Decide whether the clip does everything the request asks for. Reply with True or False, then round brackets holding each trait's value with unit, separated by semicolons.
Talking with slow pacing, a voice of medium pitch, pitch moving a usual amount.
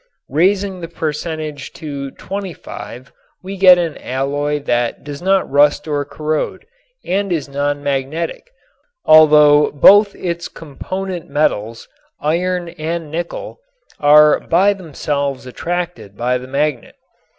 True (115 wpm; 150 Hz; 3.7 semitones)